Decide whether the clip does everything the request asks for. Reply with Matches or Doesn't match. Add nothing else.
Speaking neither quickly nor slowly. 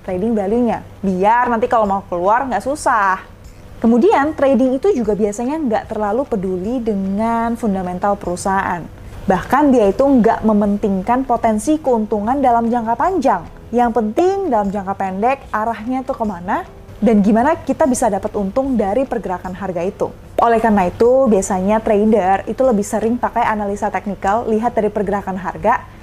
Doesn't match